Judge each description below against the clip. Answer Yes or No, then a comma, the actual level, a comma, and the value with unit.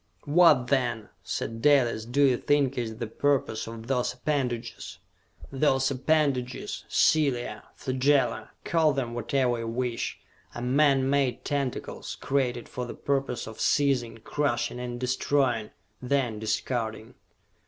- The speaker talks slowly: Yes, slow, 125 wpm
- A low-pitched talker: Yes, low, 125 Hz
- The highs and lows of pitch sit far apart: No, average, 2.9 semitones